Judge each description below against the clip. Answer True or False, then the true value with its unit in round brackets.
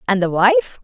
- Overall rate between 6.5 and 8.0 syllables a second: True (7.9 syllables/s)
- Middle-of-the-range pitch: True (180 Hz)